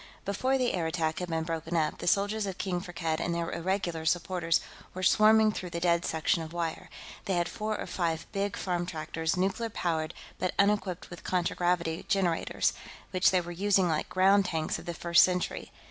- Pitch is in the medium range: Yes, medium, 175 Hz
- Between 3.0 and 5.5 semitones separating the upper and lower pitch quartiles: No, narrow, 2.6 semitones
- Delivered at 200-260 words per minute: No, average, 190 wpm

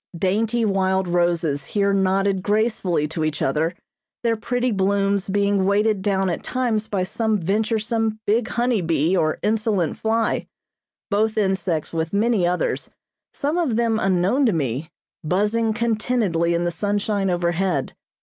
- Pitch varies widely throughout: No, average, 3.9 semitones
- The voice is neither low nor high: No, high, 200 Hz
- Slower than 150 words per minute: Yes, average, 140 wpm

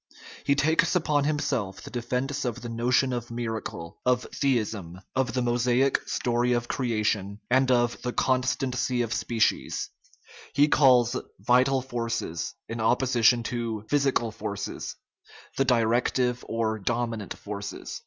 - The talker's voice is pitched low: Yes, low, 120 Hz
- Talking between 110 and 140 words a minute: Yes, slow, 135 wpm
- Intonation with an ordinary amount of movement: No, narrow, 2.2 semitones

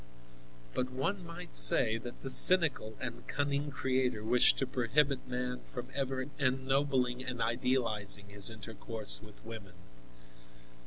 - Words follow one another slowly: Yes, slow, 125 wpm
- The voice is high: No, low, 125 Hz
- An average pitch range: Yes, average, 3.1 semitones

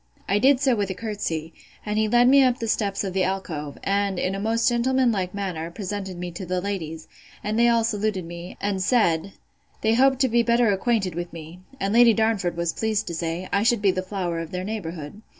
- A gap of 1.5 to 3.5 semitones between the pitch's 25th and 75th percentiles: No, average, 4.2 semitones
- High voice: Yes, high, 200 Hz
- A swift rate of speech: Yes, fast, 225 wpm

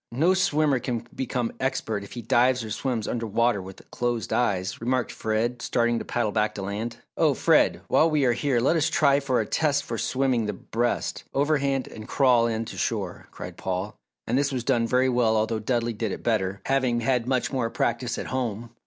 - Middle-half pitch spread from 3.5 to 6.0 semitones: No, average, 2.8 semitones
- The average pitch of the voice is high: No, low, 120 Hz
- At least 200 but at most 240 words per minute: Yes, fast, 205 wpm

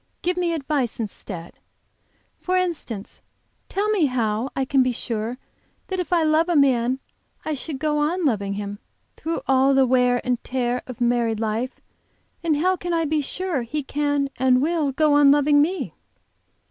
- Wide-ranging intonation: No, average, 4.5 semitones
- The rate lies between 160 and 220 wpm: Yes, average, 170 wpm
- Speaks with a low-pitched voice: No, very high, 275 Hz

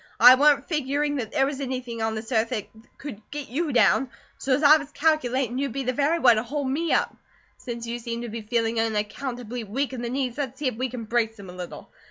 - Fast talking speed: Yes, fast, 240 wpm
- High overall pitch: Yes, very high, 255 Hz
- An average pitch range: Yes, average, 3.4 semitones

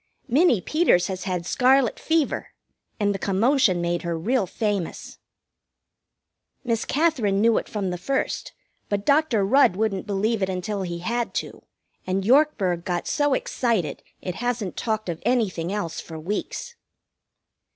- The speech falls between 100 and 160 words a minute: Yes, average, 145 wpm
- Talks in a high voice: Yes, high, 205 Hz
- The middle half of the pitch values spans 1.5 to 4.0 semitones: No, average, 5.2 semitones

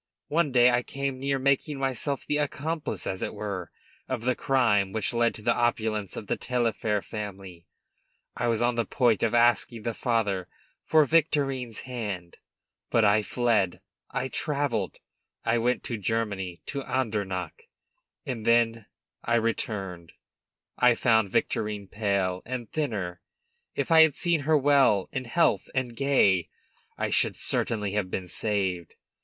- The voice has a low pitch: Yes, low, 115 Hz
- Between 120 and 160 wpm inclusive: Yes, average, 150 wpm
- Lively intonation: No, average, 4.3 semitones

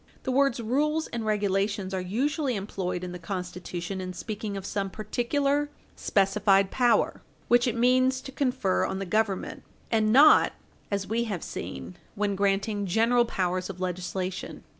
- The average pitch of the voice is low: No, high, 205 Hz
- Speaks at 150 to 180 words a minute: Yes, average, 155 wpm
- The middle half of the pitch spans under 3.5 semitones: No, average, 4.3 semitones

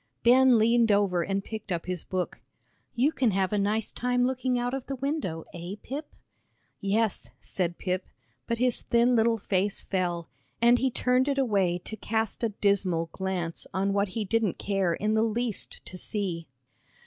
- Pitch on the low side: No, high, 210 Hz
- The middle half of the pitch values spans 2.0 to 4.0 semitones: No, average, 4.4 semitones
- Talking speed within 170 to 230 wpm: Yes, average, 175 wpm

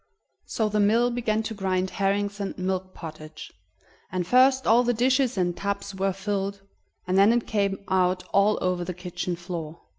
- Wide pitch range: No, average, 2.8 semitones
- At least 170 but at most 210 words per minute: Yes, average, 175 wpm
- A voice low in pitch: No, high, 195 Hz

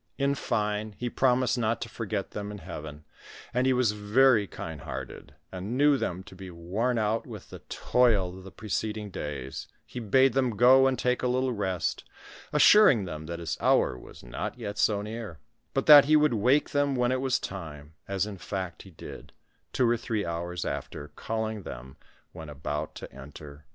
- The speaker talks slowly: No, average, 195 wpm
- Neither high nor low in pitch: No, low, 105 Hz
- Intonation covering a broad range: Yes, wide, 6.4 semitones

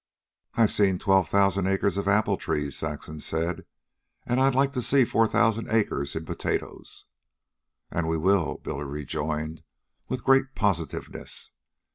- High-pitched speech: No, very low, 95 Hz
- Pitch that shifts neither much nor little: No, wide, 6.1 semitones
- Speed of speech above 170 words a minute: No, average, 140 wpm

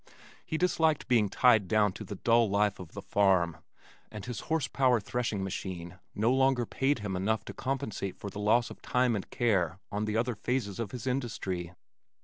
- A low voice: Yes, low, 110 Hz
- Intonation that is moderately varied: Yes, average, 4.2 semitones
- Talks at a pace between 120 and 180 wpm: No, average, 190 wpm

